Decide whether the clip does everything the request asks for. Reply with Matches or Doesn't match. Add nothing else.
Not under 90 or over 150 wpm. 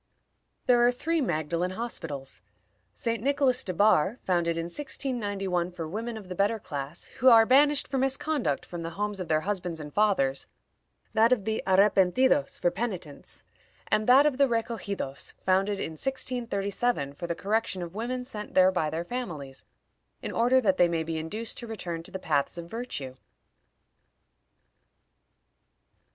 Doesn't match